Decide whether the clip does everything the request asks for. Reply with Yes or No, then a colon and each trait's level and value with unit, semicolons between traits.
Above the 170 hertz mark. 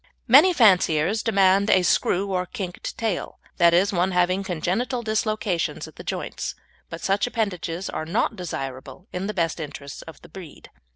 Yes: medium, 185 Hz